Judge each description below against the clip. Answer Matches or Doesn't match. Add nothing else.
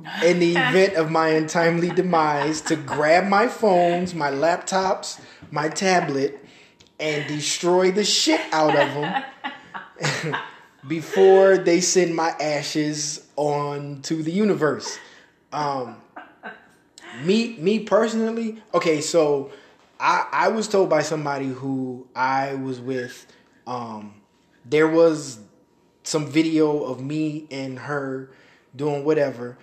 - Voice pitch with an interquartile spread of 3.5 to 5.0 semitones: Matches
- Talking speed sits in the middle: Doesn't match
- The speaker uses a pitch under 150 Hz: Doesn't match